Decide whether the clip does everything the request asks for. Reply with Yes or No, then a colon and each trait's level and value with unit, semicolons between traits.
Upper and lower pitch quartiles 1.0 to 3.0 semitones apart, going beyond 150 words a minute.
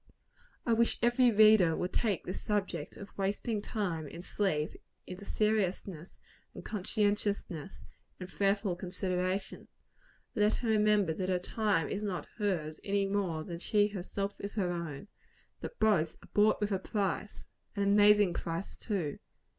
No: average, 2.7 semitones; average, 145 wpm